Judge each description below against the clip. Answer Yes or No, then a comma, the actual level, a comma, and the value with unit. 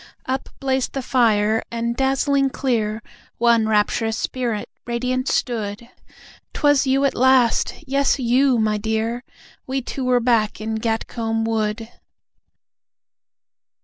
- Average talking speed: No, slow, 115 wpm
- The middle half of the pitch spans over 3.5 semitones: No, average, 2.9 semitones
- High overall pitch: Yes, high, 235 Hz